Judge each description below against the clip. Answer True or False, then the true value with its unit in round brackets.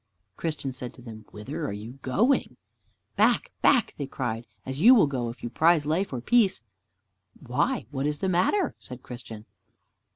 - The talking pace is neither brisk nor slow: True (170 wpm)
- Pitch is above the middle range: False (135 Hz)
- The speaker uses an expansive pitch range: True (6.5 semitones)